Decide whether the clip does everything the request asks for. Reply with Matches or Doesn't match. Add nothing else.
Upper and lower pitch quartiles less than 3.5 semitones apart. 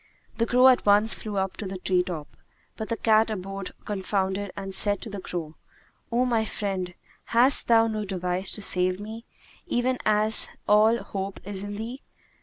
Matches